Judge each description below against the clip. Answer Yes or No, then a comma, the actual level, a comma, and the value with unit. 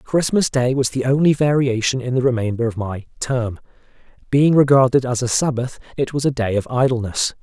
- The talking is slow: No, average, 185 wpm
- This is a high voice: No, low, 130 Hz